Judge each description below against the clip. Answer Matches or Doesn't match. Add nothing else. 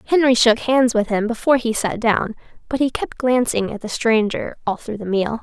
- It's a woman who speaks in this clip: Matches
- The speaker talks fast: Matches